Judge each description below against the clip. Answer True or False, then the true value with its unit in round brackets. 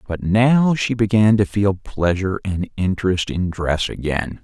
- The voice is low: True (100 Hz)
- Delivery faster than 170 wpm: False (160 wpm)